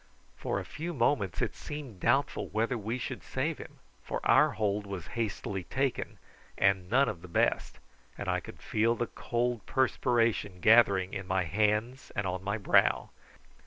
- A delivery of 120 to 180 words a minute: Yes, average, 160 wpm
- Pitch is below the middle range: Yes, low, 110 Hz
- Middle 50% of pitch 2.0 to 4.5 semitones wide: Yes, average, 3.8 semitones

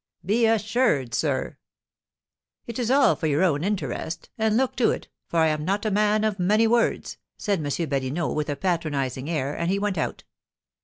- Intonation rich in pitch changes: Yes, wide, 6.1 semitones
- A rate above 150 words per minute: Yes, average, 195 wpm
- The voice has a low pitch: No, medium, 185 Hz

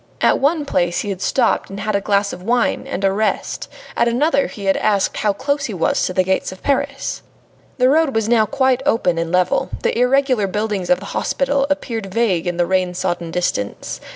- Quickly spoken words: Yes, fast, 210 wpm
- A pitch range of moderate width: No, wide, 5.9 semitones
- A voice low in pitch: No, high, 210 Hz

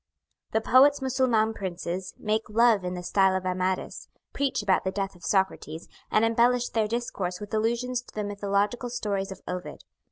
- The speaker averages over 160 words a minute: Yes, average, 170 wpm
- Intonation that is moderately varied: Yes, average, 3.9 semitones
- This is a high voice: Yes, high, 210 Hz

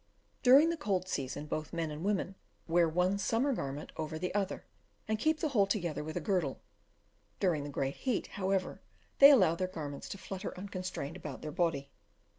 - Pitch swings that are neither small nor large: Yes, average, 4.6 semitones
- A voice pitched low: No, medium, 180 Hz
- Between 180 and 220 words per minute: Yes, average, 185 wpm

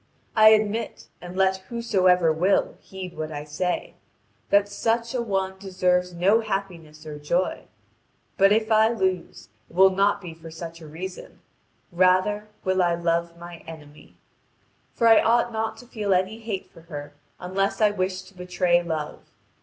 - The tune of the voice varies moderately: Yes, average, 3.4 semitones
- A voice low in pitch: No, medium, 185 Hz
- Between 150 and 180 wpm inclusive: Yes, average, 160 wpm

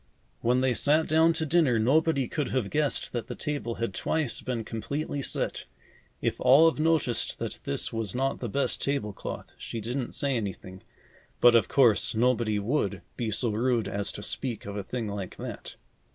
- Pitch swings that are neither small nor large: Yes, average, 4.4 semitones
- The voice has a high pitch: No, low, 125 Hz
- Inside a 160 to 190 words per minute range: Yes, average, 180 wpm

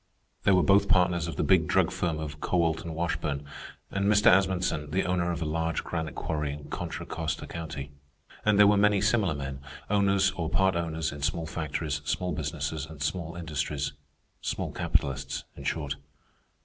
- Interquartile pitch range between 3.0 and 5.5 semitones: Yes, average, 3.6 semitones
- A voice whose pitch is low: Yes, very low, 80 Hz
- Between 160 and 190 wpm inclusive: Yes, average, 175 wpm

